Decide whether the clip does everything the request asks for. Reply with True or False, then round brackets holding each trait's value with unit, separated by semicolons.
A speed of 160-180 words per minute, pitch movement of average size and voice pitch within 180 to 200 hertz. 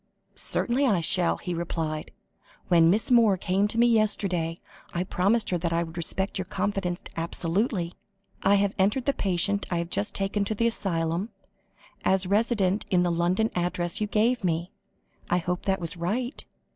True (170 wpm; 3.3 semitones; 190 Hz)